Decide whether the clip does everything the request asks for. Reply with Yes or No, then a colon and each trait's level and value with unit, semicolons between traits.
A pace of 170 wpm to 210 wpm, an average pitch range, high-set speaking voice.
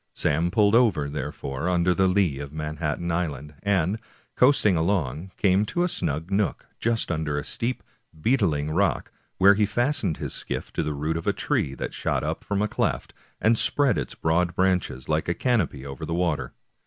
No: average, 185 wpm; average, 5.0 semitones; very low, 85 Hz